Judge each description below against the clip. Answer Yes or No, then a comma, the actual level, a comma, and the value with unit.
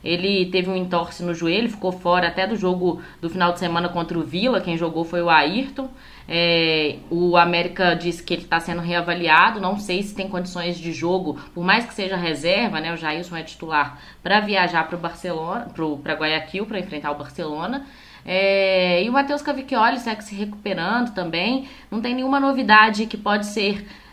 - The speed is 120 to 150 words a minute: No, fast, 185 wpm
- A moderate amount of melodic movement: Yes, average, 3.7 semitones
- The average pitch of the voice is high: No, medium, 180 Hz